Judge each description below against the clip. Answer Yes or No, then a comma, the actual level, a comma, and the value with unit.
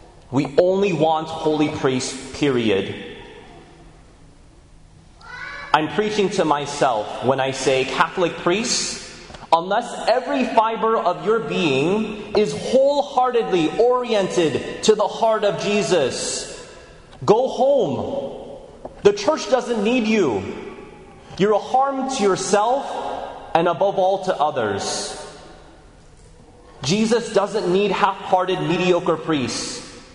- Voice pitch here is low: No, high, 200 Hz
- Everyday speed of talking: No, slow, 105 wpm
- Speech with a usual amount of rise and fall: No, wide, 6.3 semitones